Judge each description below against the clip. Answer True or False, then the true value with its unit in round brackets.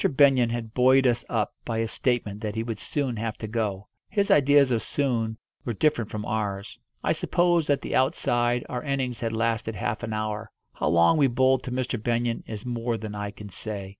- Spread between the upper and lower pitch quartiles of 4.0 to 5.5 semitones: False (3.0 semitones)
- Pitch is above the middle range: False (115 Hz)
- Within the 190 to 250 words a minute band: True (205 wpm)